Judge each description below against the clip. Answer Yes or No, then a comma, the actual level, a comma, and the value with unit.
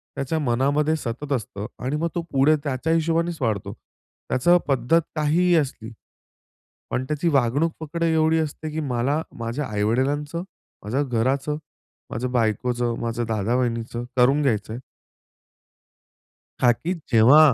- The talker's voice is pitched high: No, low, 135 Hz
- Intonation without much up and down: No, average, 4.7 semitones